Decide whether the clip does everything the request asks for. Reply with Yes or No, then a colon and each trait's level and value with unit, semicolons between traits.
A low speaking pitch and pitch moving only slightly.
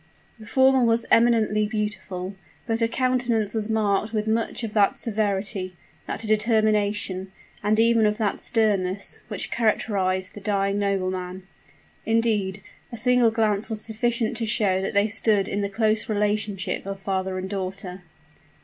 No: high, 210 Hz; narrow, 2.3 semitones